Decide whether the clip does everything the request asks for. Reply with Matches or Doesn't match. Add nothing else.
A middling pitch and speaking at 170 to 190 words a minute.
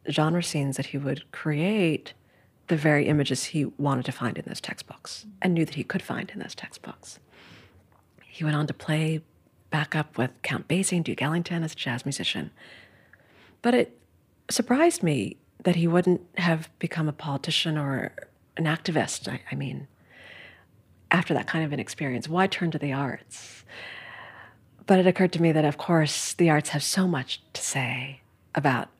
Matches